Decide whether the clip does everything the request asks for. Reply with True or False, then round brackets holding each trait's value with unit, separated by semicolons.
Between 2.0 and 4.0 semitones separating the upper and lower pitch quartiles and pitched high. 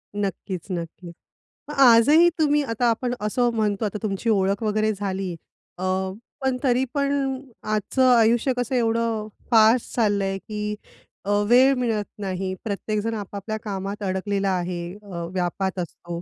True (3.6 semitones; 215 Hz)